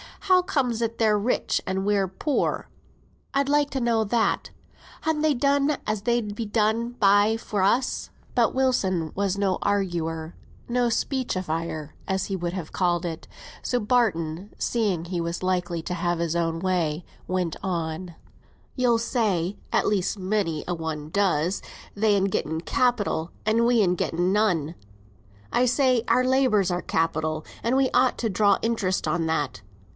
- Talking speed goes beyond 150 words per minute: Yes, average, 160 wpm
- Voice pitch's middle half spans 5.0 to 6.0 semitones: Yes, wide, 5.4 semitones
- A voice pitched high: Yes, high, 200 Hz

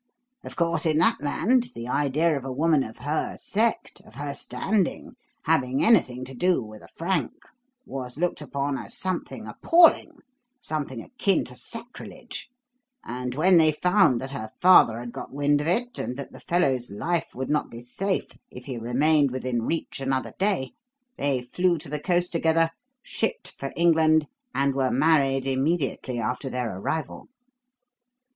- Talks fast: No, average, 165 wpm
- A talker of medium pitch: Yes, medium, 145 Hz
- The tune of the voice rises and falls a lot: No, average, 4.9 semitones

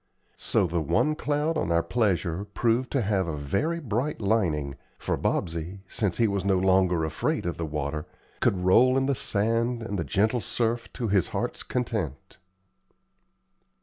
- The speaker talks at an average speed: Yes, average, 165 wpm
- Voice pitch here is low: Yes, low, 100 Hz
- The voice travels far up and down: Yes, wide, 5.7 semitones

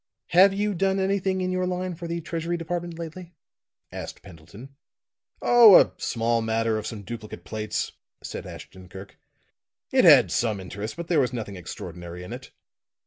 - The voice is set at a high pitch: No, medium, 150 Hz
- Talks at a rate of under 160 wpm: No, average, 165 wpm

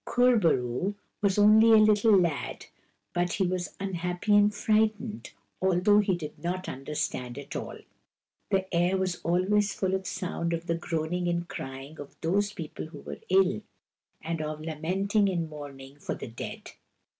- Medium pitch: Yes, medium, 180 Hz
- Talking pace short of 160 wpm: No, average, 175 wpm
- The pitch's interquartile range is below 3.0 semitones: No, average, 4.3 semitones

